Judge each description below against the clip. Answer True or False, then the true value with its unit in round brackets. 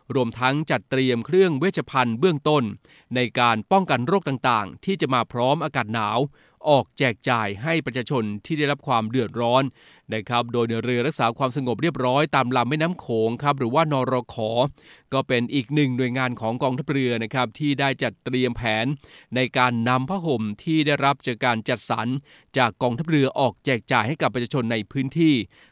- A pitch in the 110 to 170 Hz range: True (130 Hz)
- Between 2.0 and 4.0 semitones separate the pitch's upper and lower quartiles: True (3.3 semitones)